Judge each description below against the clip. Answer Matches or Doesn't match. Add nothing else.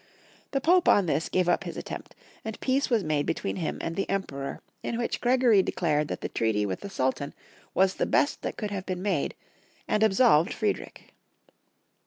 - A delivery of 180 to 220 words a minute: Matches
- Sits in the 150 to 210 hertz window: Matches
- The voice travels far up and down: Matches